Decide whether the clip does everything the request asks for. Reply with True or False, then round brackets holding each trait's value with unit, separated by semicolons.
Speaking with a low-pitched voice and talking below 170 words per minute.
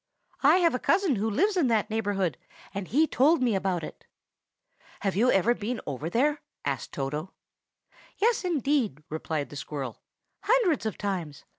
False (220 Hz; 160 wpm)